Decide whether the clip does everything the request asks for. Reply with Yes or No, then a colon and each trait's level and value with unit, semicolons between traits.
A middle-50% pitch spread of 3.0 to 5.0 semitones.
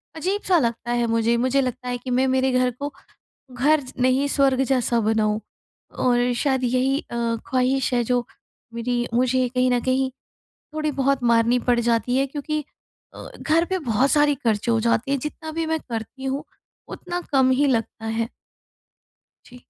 No: narrow, 2.5 semitones